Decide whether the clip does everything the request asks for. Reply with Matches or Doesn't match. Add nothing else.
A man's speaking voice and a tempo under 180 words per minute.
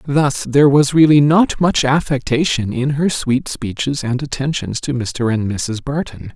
Matches